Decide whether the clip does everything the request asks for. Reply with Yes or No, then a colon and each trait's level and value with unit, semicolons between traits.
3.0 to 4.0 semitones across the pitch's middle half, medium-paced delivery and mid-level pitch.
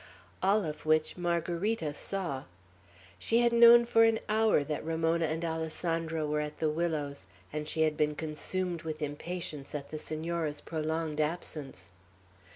No: narrow, 2.4 semitones; average, 150 wpm; medium, 160 Hz